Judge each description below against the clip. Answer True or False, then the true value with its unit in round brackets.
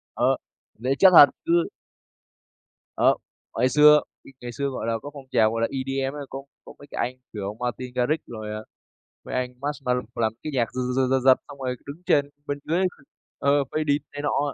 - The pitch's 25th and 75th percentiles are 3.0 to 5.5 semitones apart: False (2.6 semitones)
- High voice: False (135 Hz)